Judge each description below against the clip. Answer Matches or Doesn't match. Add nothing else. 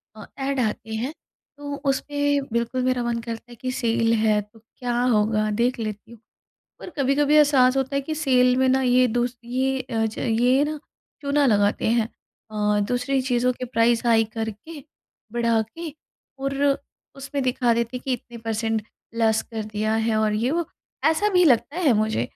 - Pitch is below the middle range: Doesn't match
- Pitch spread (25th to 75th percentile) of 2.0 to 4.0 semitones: Matches